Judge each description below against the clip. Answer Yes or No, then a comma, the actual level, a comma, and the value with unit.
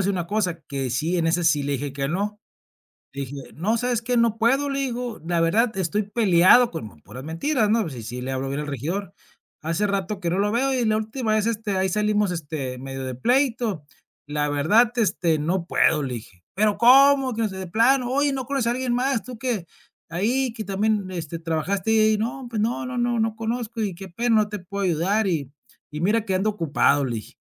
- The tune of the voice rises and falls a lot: Yes, wide, 6.2 semitones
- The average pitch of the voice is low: No, high, 200 Hz